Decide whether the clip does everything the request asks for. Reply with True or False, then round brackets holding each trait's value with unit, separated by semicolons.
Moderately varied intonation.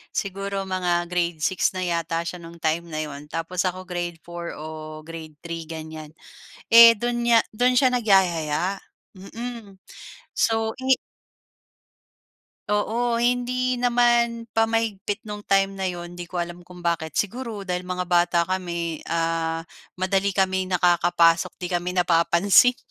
True (4.2 semitones)